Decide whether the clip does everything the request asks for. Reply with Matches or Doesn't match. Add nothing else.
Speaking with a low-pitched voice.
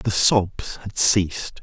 Matches